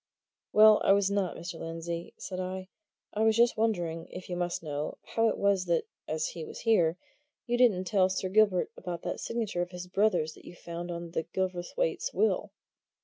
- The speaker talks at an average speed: Yes, average, 190 wpm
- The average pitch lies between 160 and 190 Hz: Yes, medium, 185 Hz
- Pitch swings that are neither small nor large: Yes, average, 3.7 semitones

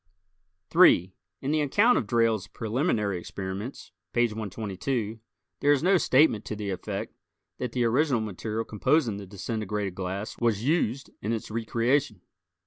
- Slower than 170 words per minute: Yes, average, 140 wpm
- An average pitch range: Yes, average, 4.2 semitones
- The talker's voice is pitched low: Yes, low, 110 Hz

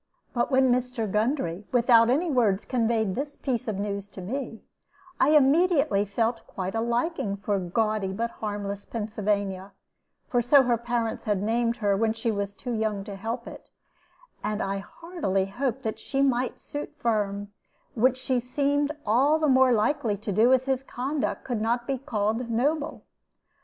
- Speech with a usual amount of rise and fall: Yes, average, 4.0 semitones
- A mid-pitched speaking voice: No, high, 230 Hz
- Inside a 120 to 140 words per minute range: No, average, 170 wpm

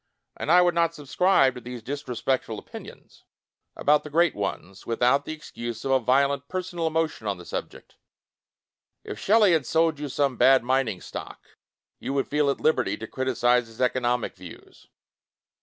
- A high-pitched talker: No, low, 135 Hz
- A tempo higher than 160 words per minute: Yes, average, 170 wpm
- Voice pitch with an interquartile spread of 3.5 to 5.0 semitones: Yes, average, 4.4 semitones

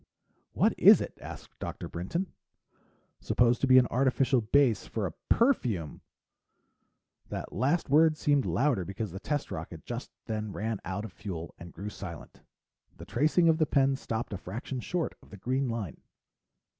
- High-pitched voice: No, low, 120 Hz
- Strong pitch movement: Yes, wide, 5.8 semitones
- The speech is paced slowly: No, average, 165 wpm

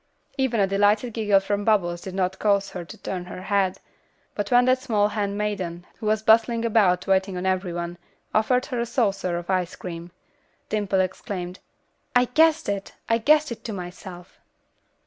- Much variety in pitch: No, average, 3.3 semitones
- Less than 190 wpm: Yes, average, 180 wpm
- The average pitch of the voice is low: No, high, 200 Hz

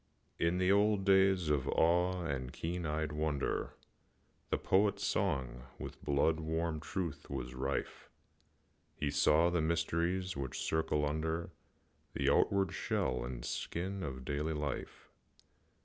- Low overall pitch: Yes, very low, 80 Hz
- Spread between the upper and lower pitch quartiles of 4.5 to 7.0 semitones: No, average, 4.0 semitones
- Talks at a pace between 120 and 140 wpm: Yes, slow, 135 wpm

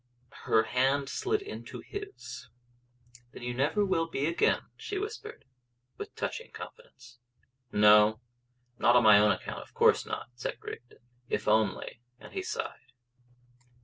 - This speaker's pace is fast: No, average, 145 wpm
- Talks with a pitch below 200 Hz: Yes, low, 135 Hz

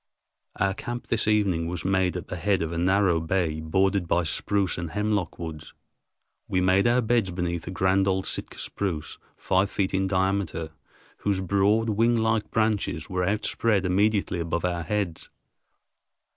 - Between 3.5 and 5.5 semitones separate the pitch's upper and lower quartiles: No, average, 2.9 semitones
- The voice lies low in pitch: Yes, very low, 95 Hz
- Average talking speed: Yes, average, 160 wpm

